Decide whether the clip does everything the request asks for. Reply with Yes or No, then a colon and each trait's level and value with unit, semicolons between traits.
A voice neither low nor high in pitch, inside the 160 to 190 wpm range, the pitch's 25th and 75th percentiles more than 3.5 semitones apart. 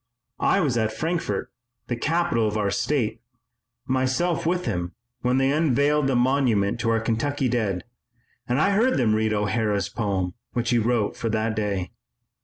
No: low, 120 Hz; average, 165 wpm; average, 4.7 semitones